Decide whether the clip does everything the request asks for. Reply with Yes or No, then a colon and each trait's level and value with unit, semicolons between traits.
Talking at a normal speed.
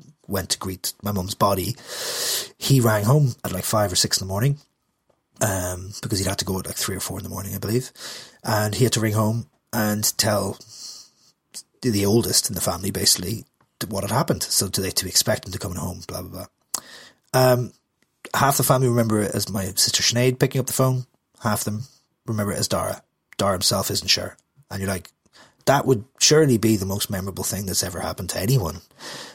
No: fast, 210 wpm